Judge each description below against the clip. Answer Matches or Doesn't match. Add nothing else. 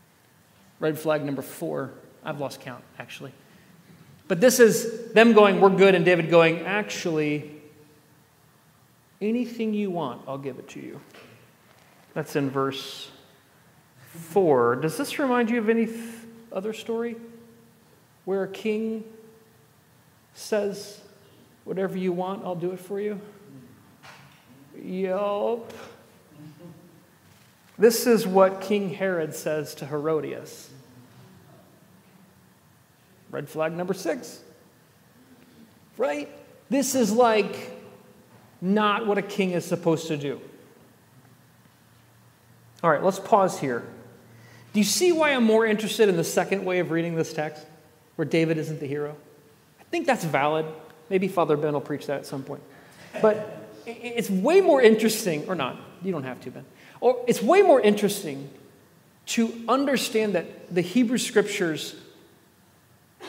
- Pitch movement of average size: Doesn't match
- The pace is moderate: Doesn't match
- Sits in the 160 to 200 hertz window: Matches